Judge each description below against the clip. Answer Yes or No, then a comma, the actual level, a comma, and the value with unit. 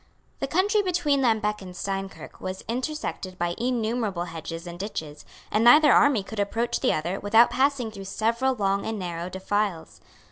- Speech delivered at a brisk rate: No, average, 165 wpm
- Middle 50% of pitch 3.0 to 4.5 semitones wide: No, average, 4.9 semitones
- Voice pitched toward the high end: Yes, high, 210 Hz